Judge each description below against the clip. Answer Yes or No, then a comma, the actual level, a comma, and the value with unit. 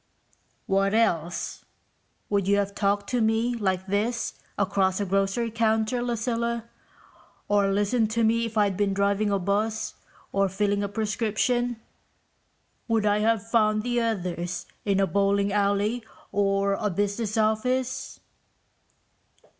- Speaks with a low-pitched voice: No, high, 205 Hz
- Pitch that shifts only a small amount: Yes, narrow, 2.3 semitones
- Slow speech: Yes, slow, 130 wpm